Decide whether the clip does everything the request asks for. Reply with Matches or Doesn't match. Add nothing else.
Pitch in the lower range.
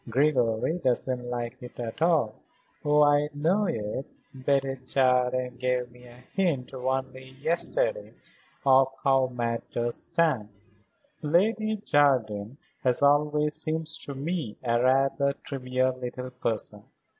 Matches